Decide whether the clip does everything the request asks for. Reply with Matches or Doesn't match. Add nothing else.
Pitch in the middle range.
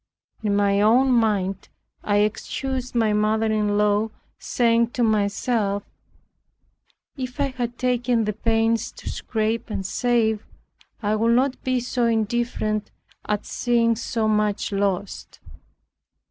Doesn't match